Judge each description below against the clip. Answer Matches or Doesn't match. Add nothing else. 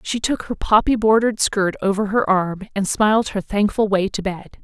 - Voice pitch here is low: Doesn't match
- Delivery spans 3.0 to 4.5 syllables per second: Doesn't match